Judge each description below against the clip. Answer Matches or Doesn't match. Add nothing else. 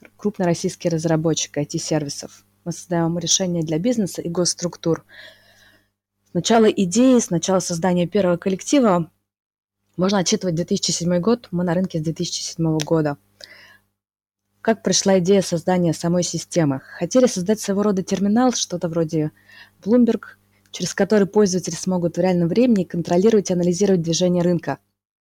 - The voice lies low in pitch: Doesn't match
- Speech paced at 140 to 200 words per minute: Doesn't match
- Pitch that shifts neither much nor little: Matches